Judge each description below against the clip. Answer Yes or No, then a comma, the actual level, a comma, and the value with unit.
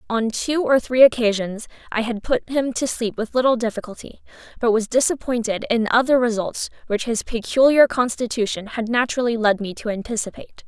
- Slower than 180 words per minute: Yes, average, 170 wpm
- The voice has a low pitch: No, high, 235 Hz